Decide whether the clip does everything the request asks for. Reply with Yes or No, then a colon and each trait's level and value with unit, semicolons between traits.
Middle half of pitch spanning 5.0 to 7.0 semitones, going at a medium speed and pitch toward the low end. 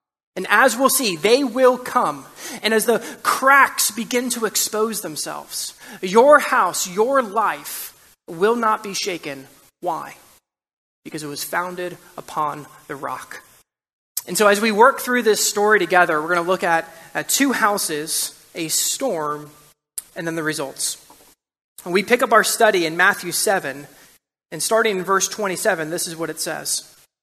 No: wide, 5.4 semitones; average, 160 wpm; high, 195 Hz